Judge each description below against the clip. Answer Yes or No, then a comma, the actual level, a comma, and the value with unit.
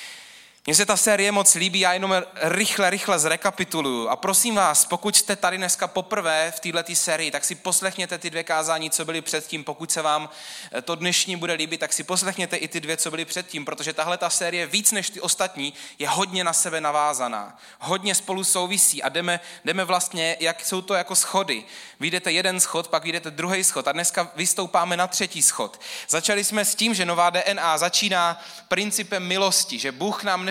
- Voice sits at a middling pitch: Yes, medium, 175 Hz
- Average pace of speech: No, fast, 195 wpm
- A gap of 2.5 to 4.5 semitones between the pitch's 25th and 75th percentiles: Yes, average, 2.8 semitones